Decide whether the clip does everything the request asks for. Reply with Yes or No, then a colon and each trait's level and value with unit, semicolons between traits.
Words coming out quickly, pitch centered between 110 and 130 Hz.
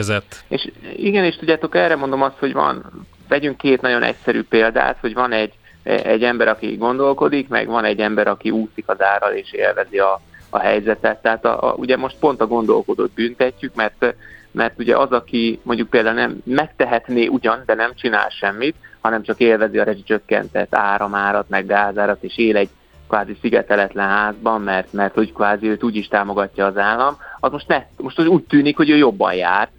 Yes: fast, 185 wpm; low, 115 Hz